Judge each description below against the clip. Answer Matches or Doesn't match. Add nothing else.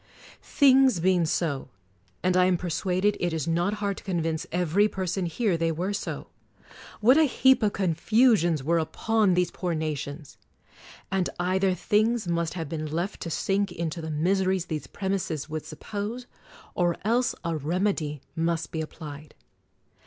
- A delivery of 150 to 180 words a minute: Matches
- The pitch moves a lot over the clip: Doesn't match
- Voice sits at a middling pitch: Matches